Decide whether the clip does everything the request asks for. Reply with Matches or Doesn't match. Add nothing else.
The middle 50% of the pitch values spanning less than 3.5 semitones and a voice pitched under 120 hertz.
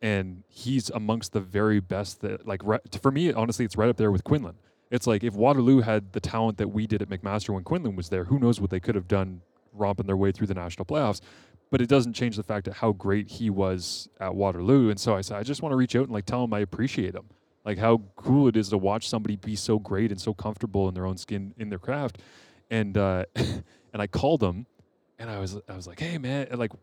Matches